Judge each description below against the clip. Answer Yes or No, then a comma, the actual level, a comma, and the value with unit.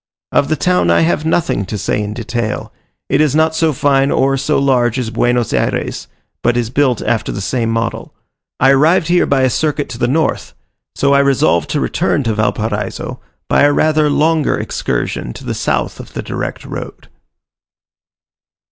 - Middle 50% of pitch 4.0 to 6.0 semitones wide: Yes, average, 4.6 semitones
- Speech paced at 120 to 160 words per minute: No, average, 180 wpm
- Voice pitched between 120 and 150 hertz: Yes, low, 135 Hz